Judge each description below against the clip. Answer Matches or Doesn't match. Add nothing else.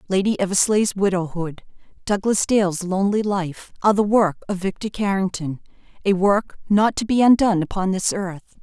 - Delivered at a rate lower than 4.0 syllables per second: Doesn't match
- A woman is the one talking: Matches